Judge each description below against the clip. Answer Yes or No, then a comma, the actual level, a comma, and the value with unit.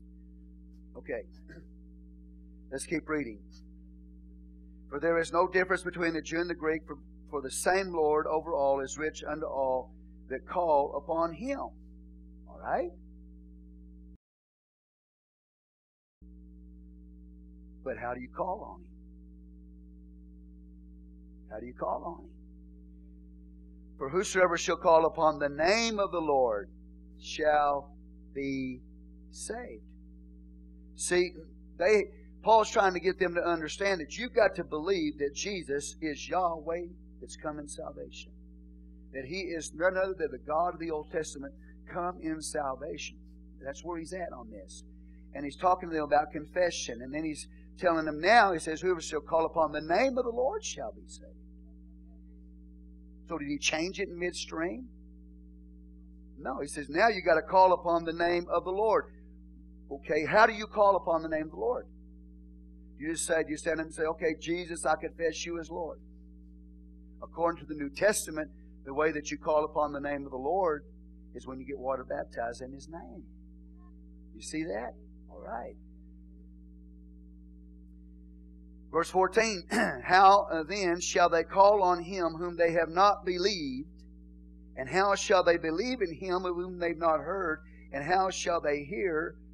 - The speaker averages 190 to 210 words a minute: No, average, 160 wpm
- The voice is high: No, medium, 140 Hz